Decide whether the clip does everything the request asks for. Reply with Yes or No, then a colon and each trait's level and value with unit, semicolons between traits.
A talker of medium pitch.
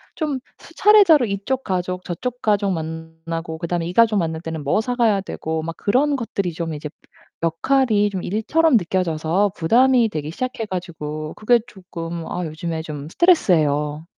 Yes: medium, 180 Hz